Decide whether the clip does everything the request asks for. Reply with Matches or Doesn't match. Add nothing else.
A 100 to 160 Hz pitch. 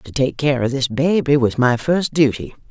Matches